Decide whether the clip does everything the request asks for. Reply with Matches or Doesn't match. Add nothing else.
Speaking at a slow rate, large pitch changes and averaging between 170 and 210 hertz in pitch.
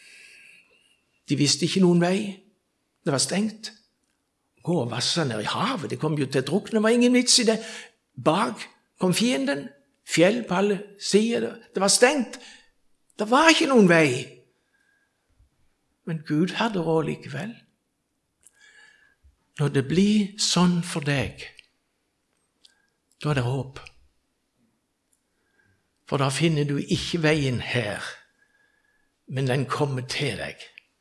Matches